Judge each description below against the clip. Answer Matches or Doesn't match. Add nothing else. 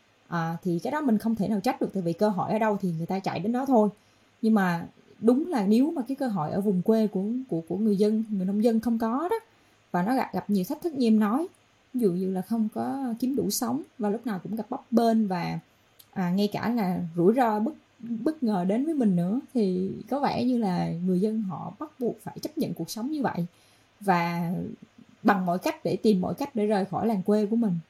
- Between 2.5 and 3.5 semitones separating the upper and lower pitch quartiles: Doesn't match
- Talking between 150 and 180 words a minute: Doesn't match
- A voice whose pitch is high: Matches